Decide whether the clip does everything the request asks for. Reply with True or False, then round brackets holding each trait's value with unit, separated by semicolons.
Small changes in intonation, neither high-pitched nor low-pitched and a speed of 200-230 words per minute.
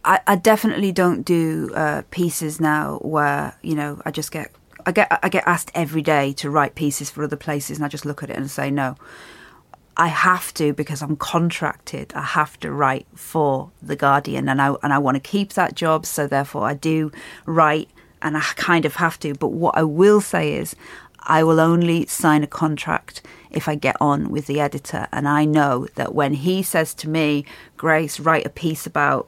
True (1.8 semitones; 155 Hz; 205 wpm)